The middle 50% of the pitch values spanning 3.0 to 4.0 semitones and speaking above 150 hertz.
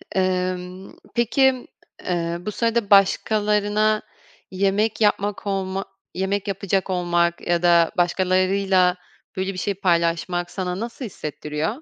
No: narrow, 2.6 semitones; high, 190 Hz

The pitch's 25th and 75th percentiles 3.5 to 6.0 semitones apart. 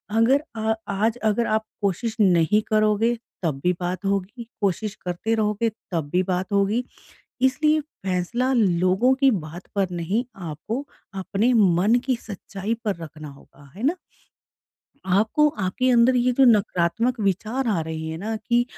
Yes: average, 4.6 semitones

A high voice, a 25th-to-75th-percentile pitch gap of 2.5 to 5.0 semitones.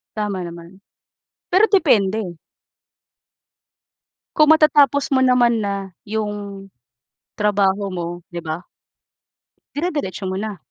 No: high, 205 Hz; wide, 5.4 semitones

